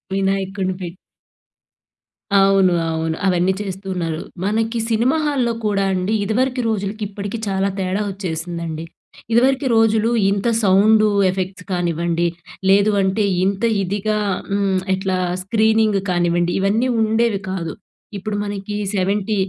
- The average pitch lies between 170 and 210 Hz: Yes, high, 195 Hz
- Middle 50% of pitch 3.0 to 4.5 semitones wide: No, narrow, 2.6 semitones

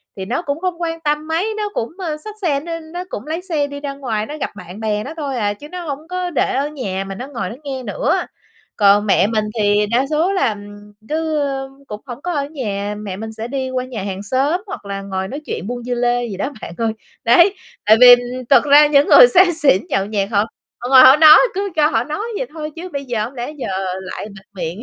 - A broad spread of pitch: Yes, wide, 6.7 semitones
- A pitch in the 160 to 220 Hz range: No, very high, 260 Hz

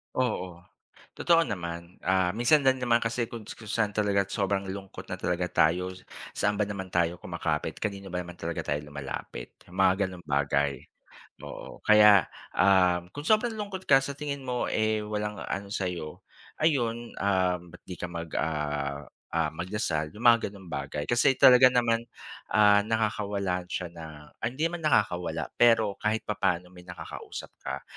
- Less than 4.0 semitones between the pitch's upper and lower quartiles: No, average, 4.6 semitones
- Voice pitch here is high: No, low, 100 Hz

